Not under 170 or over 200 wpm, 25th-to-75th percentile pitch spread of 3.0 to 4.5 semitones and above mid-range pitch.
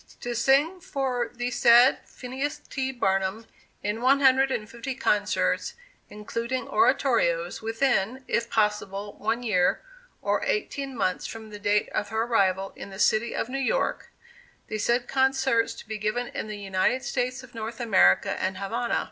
No: average, 160 wpm; average, 3.9 semitones; high, 235 Hz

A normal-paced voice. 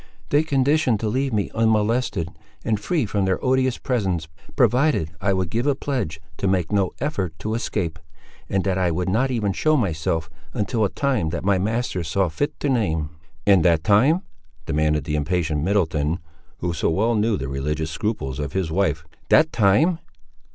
Yes: average, 175 wpm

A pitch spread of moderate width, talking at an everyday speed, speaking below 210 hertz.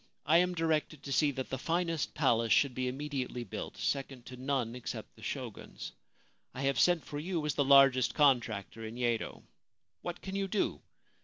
Yes: average, 3.8 semitones; average, 180 wpm; medium, 140 Hz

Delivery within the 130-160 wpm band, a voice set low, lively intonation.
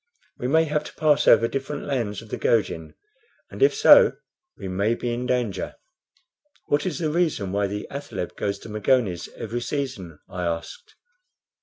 No: average, 170 wpm; low, 120 Hz; wide, 6.3 semitones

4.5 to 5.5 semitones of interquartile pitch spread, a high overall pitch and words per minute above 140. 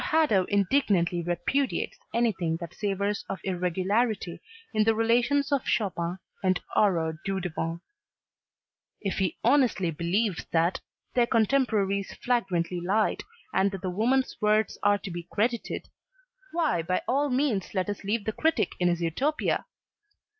No: average, 4.8 semitones; high, 200 Hz; slow, 135 wpm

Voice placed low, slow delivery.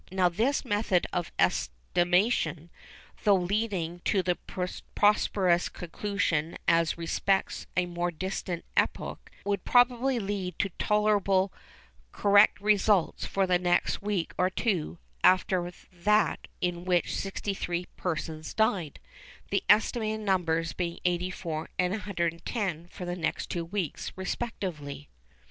No: medium, 185 Hz; slow, 115 wpm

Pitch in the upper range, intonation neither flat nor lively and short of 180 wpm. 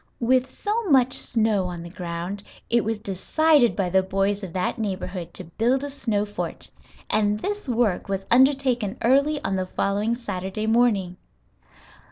Yes: high, 215 Hz; average, 4.9 semitones; average, 160 wpm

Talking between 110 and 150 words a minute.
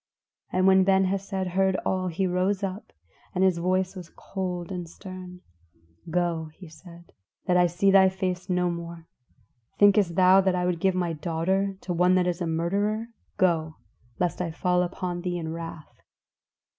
No: average, 170 wpm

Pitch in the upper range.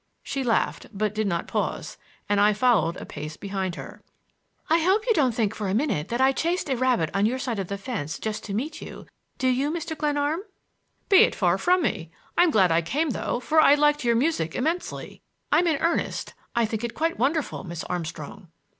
Yes: high, 240 Hz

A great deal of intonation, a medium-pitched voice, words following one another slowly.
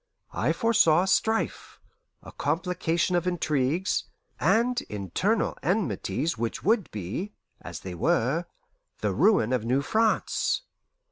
Yes: wide, 8.5 semitones; medium, 175 Hz; slow, 120 wpm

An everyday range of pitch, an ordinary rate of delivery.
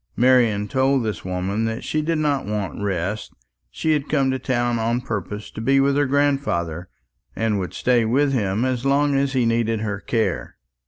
Yes: average, 4.6 semitones; average, 190 wpm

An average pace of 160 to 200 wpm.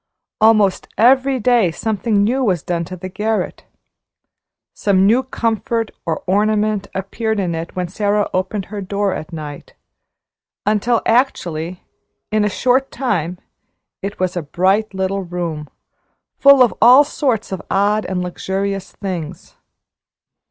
No: slow, 135 wpm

